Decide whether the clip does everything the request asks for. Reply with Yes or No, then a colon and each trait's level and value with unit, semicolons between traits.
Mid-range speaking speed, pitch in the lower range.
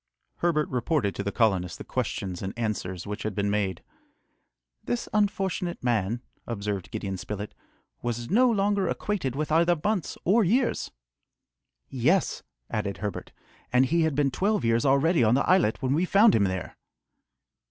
Yes: average, 155 wpm; low, 130 Hz